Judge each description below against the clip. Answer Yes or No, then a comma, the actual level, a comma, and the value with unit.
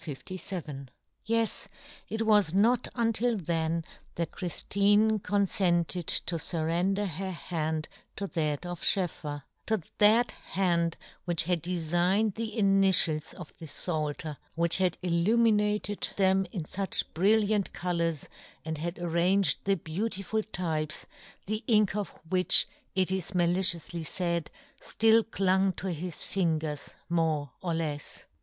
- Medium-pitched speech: Yes, medium, 180 Hz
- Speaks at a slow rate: Yes, slow, 130 wpm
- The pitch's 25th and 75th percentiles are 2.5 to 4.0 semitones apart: Yes, average, 3.5 semitones